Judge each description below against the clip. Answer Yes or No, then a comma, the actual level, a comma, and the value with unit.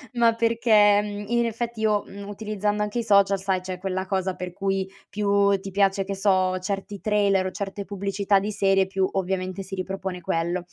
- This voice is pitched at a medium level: No, high, 195 Hz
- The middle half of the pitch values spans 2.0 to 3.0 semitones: No, narrow, 1.5 semitones